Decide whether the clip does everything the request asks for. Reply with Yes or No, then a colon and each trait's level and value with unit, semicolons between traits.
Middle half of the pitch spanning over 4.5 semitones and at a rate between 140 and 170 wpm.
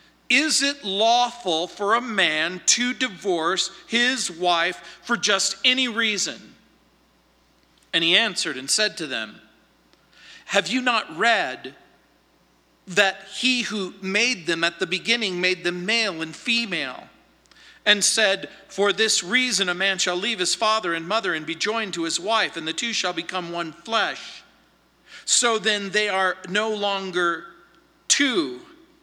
Yes: average, 4.9 semitones; average, 145 wpm